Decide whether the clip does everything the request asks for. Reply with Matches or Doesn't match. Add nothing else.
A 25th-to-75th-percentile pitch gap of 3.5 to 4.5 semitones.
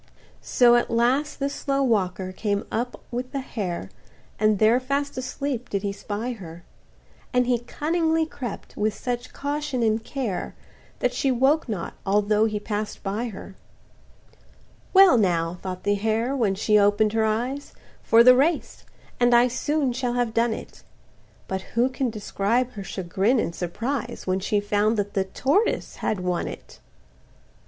Matches